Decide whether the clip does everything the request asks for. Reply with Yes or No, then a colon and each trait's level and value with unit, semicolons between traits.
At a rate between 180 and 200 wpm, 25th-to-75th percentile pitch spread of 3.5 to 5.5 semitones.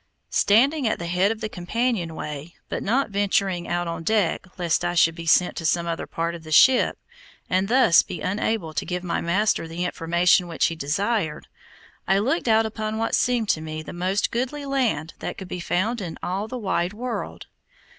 Yes: average, 195 wpm; average, 4.6 semitones